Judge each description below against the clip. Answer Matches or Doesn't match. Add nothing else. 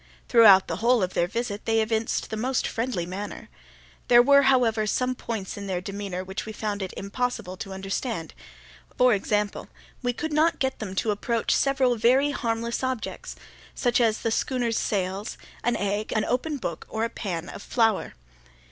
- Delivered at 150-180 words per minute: Matches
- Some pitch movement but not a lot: Matches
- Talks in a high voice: Matches